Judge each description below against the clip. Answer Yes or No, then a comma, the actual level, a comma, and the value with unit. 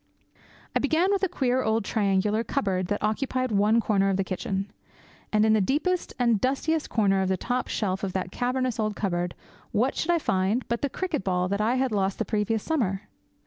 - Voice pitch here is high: Yes, high, 215 Hz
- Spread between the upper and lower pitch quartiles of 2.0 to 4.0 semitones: No, average, 4.8 semitones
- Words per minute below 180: No, fast, 205 wpm